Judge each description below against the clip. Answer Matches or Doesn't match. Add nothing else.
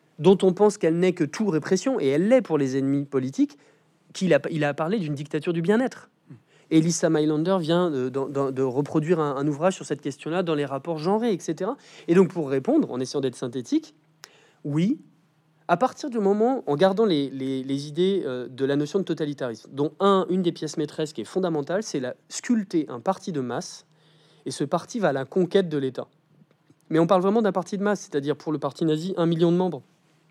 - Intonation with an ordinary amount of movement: Matches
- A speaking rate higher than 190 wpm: Matches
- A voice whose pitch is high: Doesn't match